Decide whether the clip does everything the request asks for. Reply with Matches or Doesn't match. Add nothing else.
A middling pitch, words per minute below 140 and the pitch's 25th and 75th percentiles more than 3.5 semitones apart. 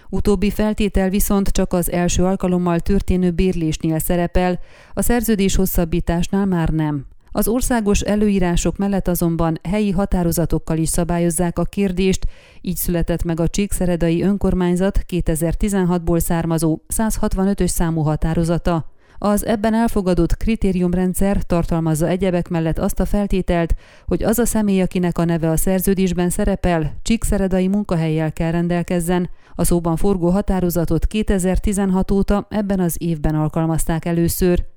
Doesn't match